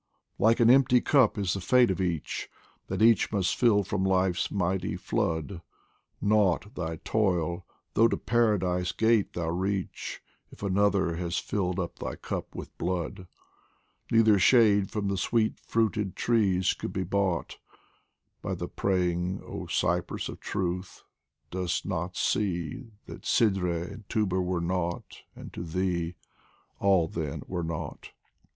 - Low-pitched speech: Yes, very low, 95 Hz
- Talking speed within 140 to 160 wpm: Yes, average, 145 wpm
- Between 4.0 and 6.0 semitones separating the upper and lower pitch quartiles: No, average, 3.0 semitones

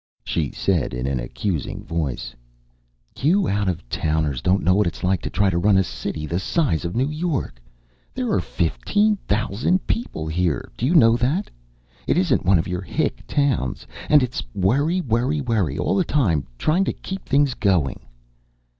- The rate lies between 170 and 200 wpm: Yes, average, 180 wpm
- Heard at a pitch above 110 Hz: No, low, 100 Hz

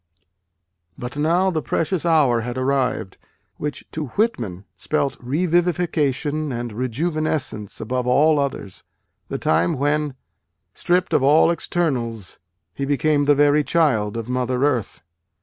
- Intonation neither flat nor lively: Yes, average, 4.2 semitones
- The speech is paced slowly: Yes, slow, 125 wpm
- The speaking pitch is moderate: Yes, medium, 145 Hz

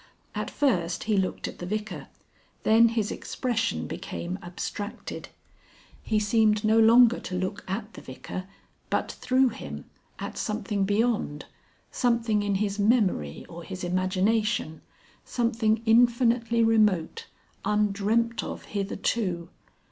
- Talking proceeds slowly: Yes, slow, 120 wpm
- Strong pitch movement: No, average, 3.4 semitones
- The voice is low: No, high, 215 Hz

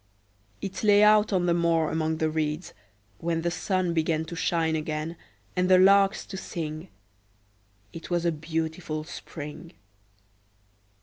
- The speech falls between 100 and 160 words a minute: Yes, average, 140 wpm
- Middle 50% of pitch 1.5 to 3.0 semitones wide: Yes, narrow, 2.4 semitones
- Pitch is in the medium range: Yes, medium, 165 Hz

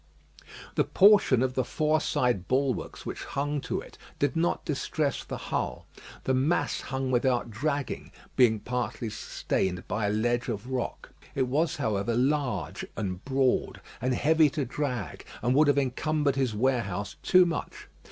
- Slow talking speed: No, average, 155 wpm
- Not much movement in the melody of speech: No, average, 3.6 semitones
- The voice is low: Yes, low, 130 Hz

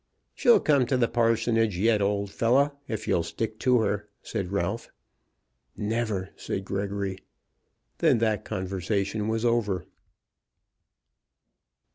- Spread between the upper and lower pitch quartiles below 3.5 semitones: Yes, average, 2.8 semitones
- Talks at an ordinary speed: No, slow, 115 wpm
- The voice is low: Yes, low, 110 Hz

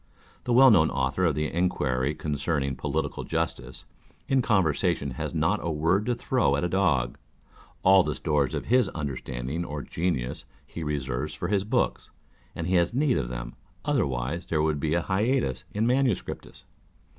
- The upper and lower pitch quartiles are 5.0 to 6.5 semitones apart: Yes, wide, 5.6 semitones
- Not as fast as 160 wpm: No, average, 165 wpm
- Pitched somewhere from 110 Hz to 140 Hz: No, very low, 80 Hz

